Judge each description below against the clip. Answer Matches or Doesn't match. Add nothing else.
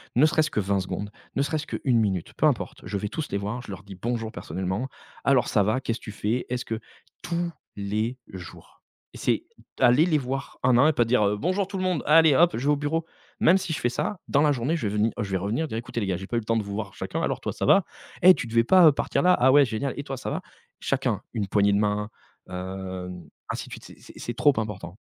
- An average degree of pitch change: Doesn't match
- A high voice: Doesn't match